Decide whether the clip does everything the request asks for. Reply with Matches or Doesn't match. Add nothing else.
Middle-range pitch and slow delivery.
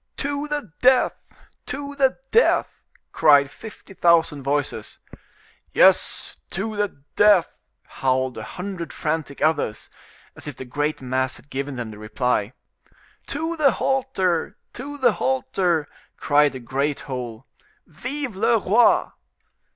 Matches